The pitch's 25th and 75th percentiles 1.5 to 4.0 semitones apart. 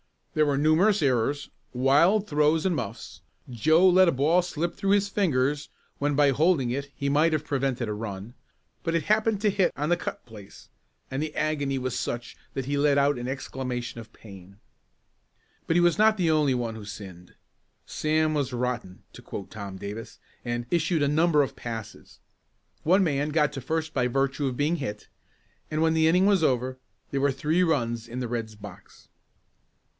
No: average, 4.8 semitones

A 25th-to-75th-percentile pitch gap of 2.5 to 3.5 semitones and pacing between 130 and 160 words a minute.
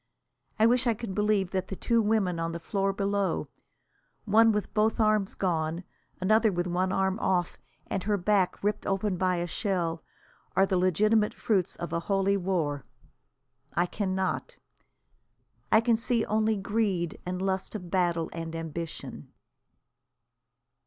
Yes: average, 3.2 semitones; average, 150 wpm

